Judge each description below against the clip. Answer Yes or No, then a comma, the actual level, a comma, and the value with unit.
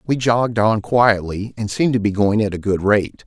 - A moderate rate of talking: No, fast, 220 wpm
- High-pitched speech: No, low, 110 Hz